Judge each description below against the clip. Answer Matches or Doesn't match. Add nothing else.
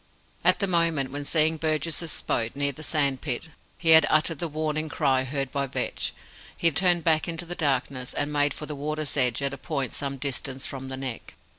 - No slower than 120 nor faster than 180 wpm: Doesn't match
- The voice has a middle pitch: Matches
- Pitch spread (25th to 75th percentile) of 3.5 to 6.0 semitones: Doesn't match